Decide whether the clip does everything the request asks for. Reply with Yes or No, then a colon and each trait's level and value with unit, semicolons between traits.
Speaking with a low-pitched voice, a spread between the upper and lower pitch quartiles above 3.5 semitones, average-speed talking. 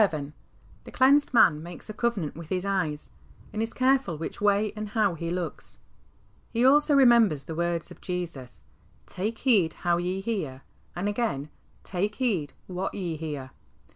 No: medium, 185 Hz; wide, 5.4 semitones; average, 165 wpm